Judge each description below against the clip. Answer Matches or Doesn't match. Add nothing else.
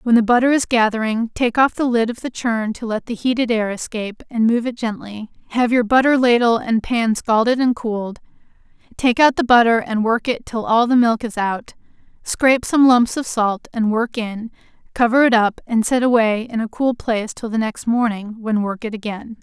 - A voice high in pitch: Matches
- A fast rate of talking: Matches